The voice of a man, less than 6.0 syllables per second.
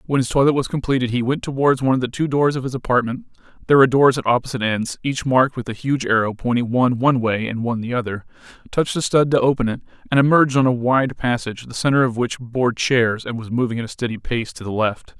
No: male; 6.6 syllables/s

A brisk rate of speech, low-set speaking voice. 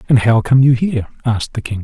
Yes: fast, 260 wpm; low, 120 Hz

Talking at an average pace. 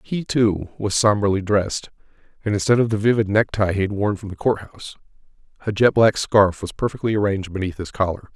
Yes: average, 195 wpm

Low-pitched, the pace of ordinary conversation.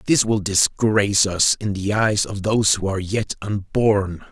Yes: low, 100 Hz; average, 180 wpm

